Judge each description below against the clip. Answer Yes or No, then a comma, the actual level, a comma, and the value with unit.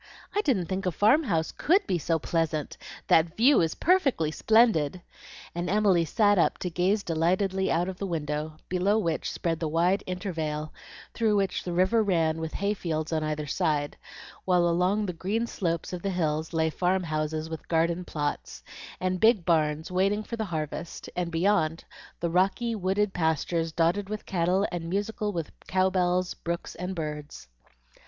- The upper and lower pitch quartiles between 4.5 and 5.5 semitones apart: No, average, 3.4 semitones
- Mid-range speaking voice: Yes, medium, 175 Hz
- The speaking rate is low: No, average, 175 wpm